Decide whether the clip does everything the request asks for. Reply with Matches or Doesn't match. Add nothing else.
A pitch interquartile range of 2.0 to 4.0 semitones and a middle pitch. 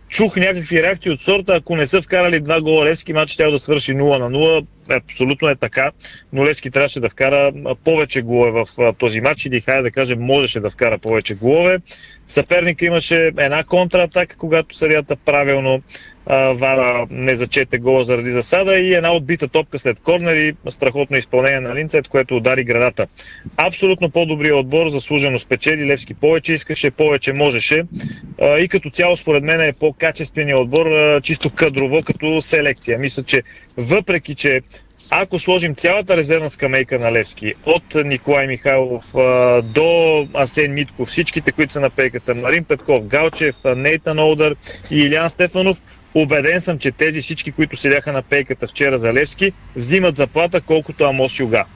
Matches